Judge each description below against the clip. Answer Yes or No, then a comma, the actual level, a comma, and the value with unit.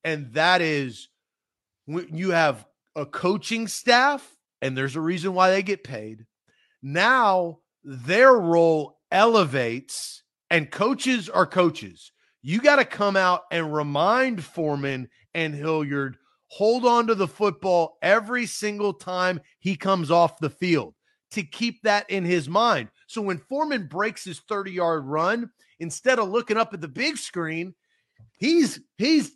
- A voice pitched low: No, medium, 180 Hz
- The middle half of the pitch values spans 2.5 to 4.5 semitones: No, average, 5.1 semitones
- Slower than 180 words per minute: Yes, average, 145 wpm